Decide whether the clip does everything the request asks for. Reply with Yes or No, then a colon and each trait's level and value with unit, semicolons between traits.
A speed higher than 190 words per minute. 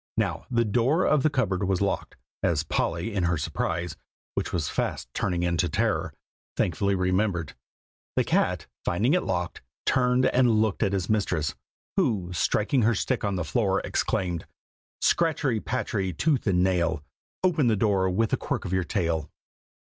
No: average, 165 wpm